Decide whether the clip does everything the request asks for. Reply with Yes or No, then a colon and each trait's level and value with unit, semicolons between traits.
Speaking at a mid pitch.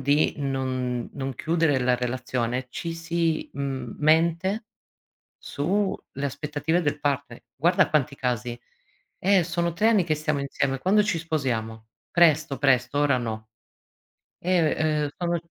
Yes: medium, 145 Hz